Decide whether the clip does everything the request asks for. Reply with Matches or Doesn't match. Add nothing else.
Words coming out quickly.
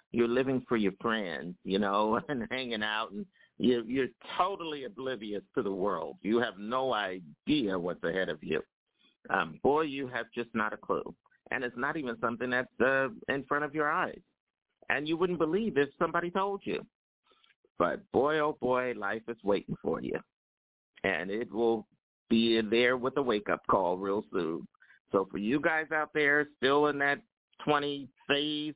Doesn't match